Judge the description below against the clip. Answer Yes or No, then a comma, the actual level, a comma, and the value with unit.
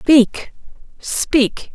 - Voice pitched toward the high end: Yes, very high, 255 Hz